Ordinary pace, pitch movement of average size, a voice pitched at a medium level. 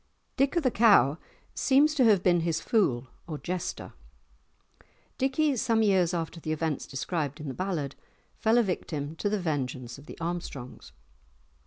No: average, 160 wpm; wide, 7.0 semitones; medium, 175 Hz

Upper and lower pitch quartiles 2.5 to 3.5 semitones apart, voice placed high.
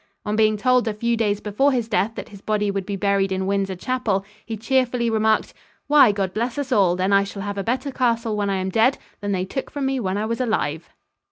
Yes: average, 3.2 semitones; high, 215 Hz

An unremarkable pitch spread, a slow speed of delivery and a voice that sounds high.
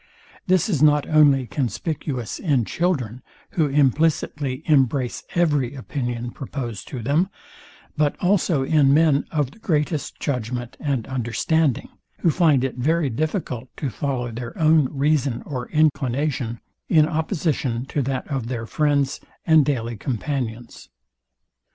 No: average, 3.7 semitones; slow, 130 wpm; medium, 140 Hz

